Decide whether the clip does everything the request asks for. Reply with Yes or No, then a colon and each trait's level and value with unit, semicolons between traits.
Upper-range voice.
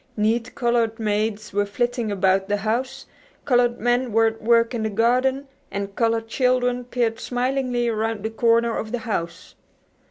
Yes: high, 230 Hz